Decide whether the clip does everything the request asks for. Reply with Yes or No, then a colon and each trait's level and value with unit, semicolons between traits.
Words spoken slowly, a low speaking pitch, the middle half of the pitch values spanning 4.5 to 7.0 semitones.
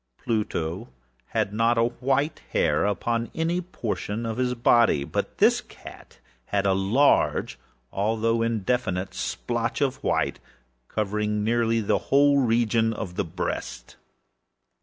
No: slow, 125 wpm; low, 115 Hz; average, 2.8 semitones